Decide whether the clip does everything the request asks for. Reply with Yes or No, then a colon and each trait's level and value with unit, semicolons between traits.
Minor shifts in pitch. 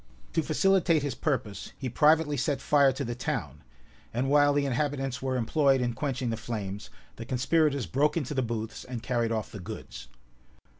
No: average, 3.9 semitones